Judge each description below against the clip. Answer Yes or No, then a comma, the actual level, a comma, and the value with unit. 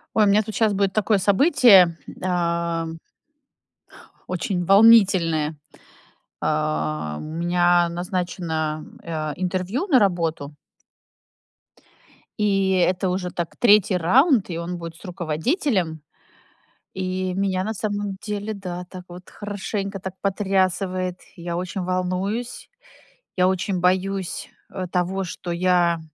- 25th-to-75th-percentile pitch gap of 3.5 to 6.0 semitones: No, narrow, 2.5 semitones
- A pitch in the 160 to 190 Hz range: Yes, medium, 185 Hz